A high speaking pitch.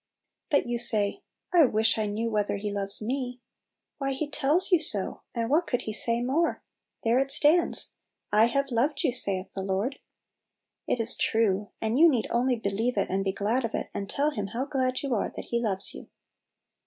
Yes: high, 235 Hz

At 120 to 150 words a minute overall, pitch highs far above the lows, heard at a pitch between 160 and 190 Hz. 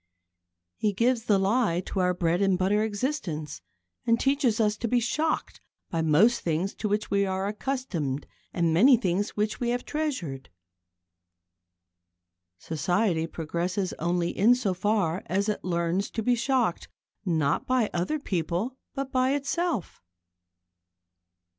No: average, 140 wpm; wide, 5.8 semitones; high, 200 Hz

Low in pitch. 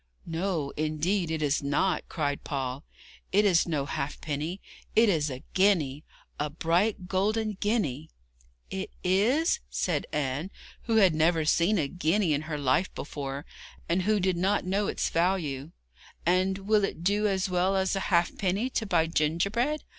No: medium, 175 Hz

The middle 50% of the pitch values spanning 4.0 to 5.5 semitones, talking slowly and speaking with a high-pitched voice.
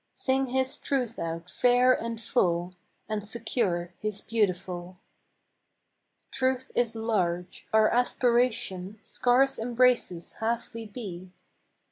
Yes: average, 5.2 semitones; slow, 105 wpm; high, 225 Hz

